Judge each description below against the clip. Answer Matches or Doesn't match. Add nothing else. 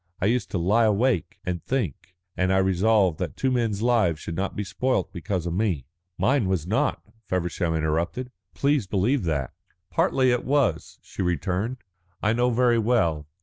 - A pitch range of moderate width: Doesn't match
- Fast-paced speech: Doesn't match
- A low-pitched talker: Matches